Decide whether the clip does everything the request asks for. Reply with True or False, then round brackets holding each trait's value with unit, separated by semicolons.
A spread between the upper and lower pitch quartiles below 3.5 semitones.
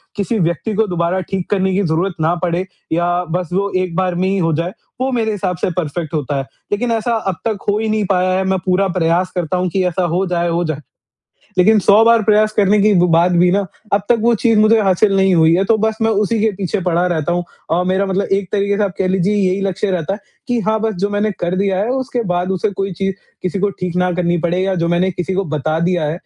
True (2.9 semitones)